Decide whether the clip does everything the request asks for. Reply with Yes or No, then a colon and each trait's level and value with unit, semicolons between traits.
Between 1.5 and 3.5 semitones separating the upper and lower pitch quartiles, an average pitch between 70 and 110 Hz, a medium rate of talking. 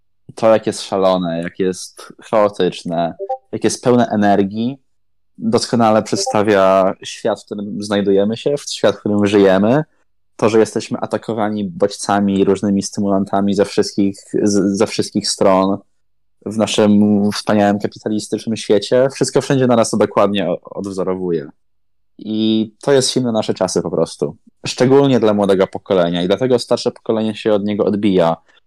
Yes: narrow, 2.4 semitones; low, 105 Hz; average, 140 wpm